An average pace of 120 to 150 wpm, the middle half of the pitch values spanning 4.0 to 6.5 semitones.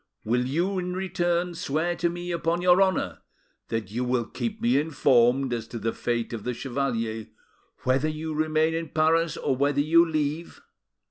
No: average, 175 wpm; wide, 5.4 semitones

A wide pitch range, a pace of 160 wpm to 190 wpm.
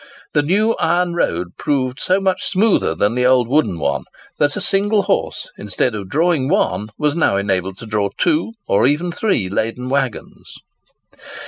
Yes: wide, 9.0 semitones; average, 165 wpm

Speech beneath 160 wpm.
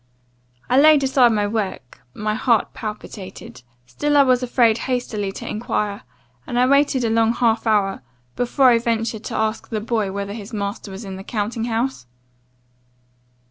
No: average, 165 wpm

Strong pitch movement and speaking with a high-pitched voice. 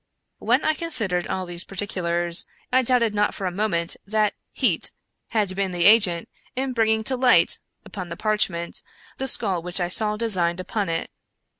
No: average, 4.0 semitones; high, 200 Hz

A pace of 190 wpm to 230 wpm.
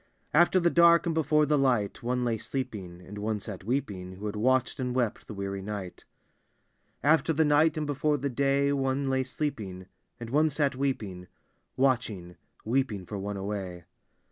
No: average, 175 wpm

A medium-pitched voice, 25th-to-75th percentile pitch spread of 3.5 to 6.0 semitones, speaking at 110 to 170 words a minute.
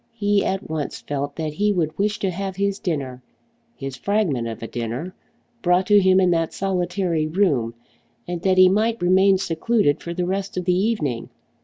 No: medium, 180 Hz; average, 4.2 semitones; average, 185 wpm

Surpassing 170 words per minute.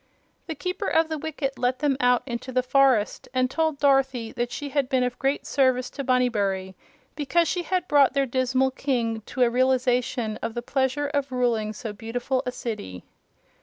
Yes: average, 185 wpm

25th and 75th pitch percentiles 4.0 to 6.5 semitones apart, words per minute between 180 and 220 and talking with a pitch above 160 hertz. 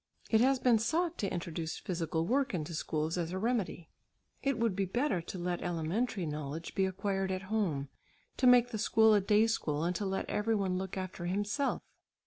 Yes: average, 4.6 semitones; average, 195 wpm; high, 190 Hz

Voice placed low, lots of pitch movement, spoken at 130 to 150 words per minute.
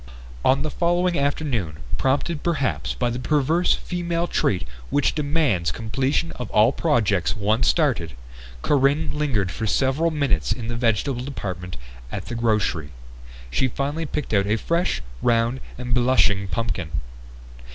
Yes: low, 125 Hz; wide, 5.8 semitones; average, 140 wpm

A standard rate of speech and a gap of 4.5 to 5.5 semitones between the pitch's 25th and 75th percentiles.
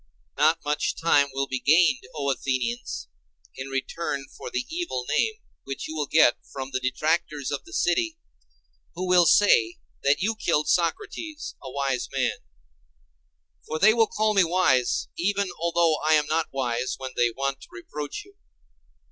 Yes: average, 165 wpm; average, 5.0 semitones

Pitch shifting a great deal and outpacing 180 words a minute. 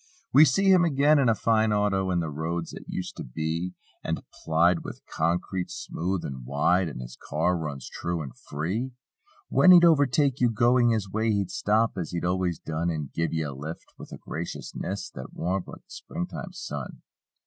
Yes: wide, 6.2 semitones; average, 190 wpm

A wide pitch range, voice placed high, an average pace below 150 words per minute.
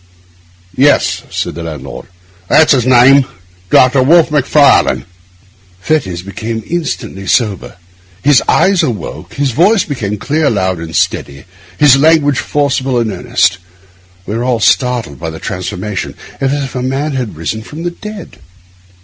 No: wide, 6.6 semitones; low, 125 Hz; average, 140 wpm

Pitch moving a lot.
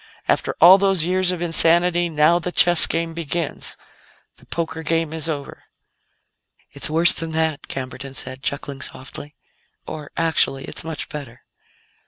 No: average, 2.7 semitones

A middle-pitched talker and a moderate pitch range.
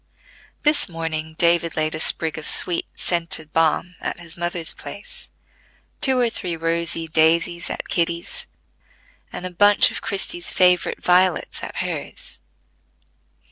No: medium, 170 Hz; narrow, 1.9 semitones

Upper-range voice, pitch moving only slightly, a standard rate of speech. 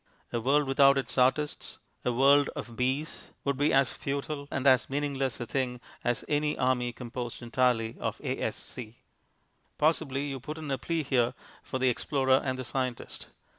No: low, 130 Hz; narrow, 2.3 semitones; average, 170 wpm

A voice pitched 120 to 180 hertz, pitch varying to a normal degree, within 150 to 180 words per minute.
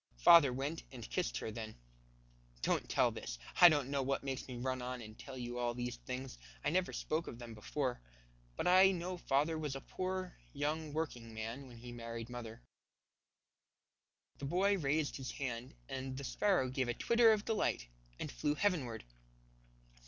Yes: low, 135 Hz; average, 4.8 semitones; average, 175 wpm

